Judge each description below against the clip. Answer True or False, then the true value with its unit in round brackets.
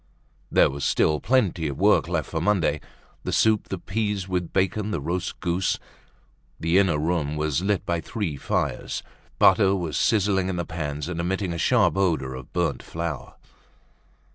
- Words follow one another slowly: False (165 wpm)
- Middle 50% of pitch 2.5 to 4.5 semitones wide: True (3.7 semitones)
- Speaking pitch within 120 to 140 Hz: False (90 Hz)